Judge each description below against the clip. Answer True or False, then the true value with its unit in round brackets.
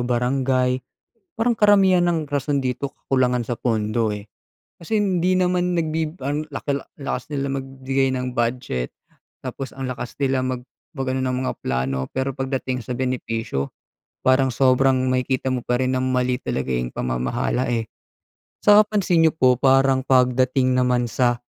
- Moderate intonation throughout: False (1.9 semitones)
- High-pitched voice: False (130 Hz)